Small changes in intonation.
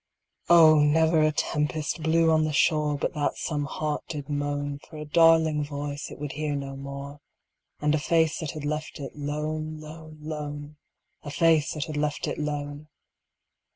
Yes: narrow, 1.3 semitones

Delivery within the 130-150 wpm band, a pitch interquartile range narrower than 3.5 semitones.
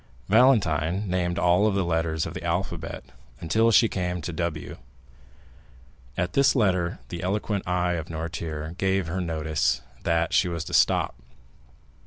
Yes: average, 145 wpm; average, 2.8 semitones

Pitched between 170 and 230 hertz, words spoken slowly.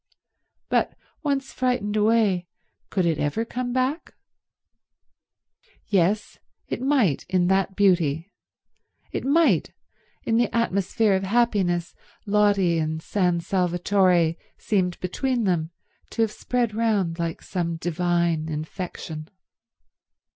Yes: high, 190 Hz; slow, 105 wpm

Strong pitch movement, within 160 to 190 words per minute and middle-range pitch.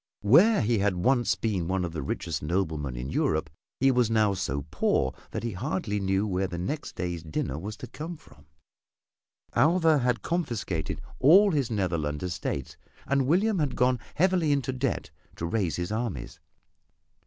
No: wide, 8.0 semitones; average, 165 wpm; low, 105 Hz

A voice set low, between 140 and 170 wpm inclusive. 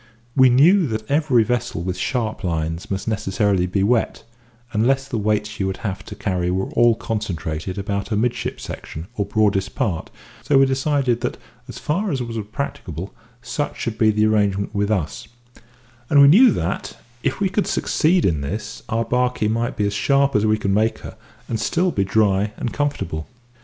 No: low, 110 Hz; average, 185 wpm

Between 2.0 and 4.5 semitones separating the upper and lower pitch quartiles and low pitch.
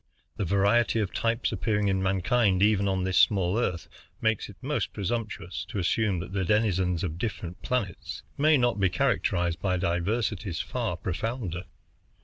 Yes: average, 3.6 semitones; low, 100 Hz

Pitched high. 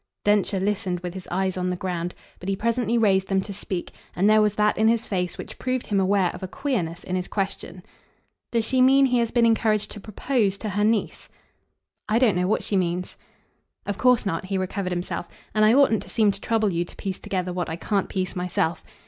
Yes: high, 200 Hz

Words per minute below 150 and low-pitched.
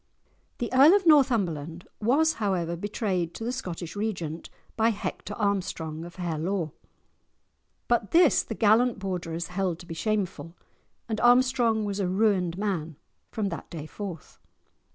No: average, 140 wpm; high, 200 Hz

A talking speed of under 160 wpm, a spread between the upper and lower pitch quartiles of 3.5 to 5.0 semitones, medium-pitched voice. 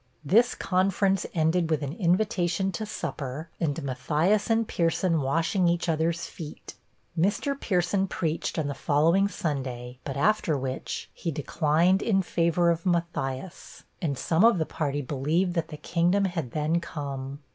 Yes: average, 150 wpm; average, 3.9 semitones; medium, 165 Hz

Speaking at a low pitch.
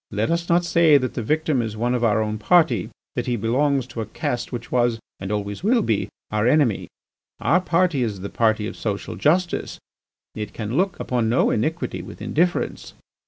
Yes: low, 120 Hz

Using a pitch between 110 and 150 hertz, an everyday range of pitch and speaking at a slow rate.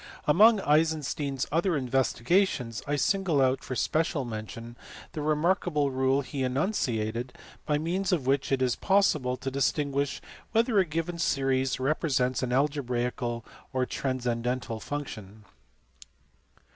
Yes: low, 135 Hz; average, 3.7 semitones; slow, 130 wpm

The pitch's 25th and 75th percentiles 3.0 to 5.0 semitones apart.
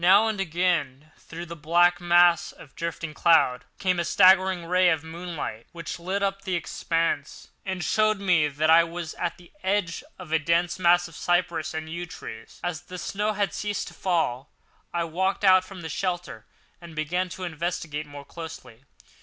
No: narrow, 2.4 semitones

